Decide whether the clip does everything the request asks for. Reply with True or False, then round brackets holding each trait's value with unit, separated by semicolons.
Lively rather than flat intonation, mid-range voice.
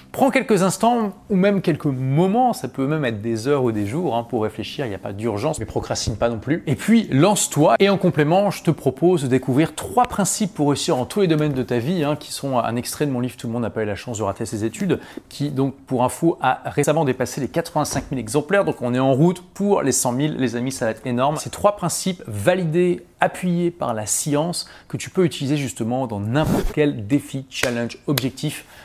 True (5.8 semitones; 145 Hz)